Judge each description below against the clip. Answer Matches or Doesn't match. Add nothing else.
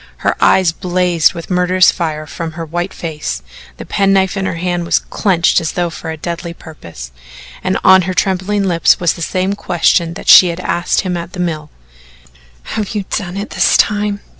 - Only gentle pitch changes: Matches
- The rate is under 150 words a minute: Doesn't match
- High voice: Doesn't match